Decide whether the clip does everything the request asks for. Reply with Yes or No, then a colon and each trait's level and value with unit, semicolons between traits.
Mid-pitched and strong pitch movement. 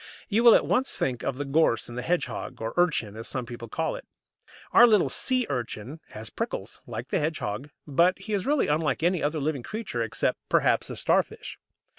Yes: medium, 150 Hz; wide, 7.2 semitones